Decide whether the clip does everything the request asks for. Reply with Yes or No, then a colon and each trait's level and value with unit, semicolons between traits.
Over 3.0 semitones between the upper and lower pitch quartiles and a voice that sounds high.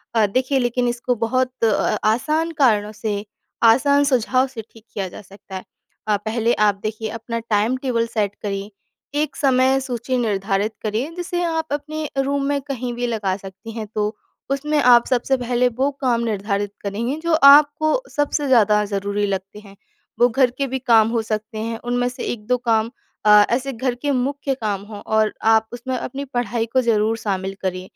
Yes: average, 3.7 semitones; high, 235 Hz